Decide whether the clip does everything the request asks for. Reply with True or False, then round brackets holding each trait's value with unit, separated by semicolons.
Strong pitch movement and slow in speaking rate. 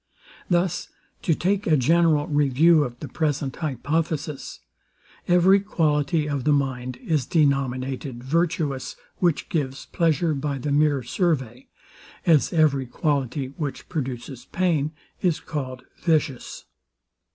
False (3.6 semitones; 120 wpm)